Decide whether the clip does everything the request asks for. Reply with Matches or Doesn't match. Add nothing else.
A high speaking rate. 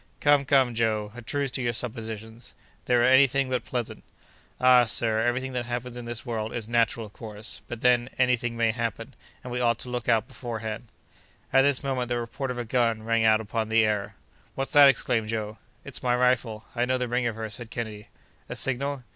Matches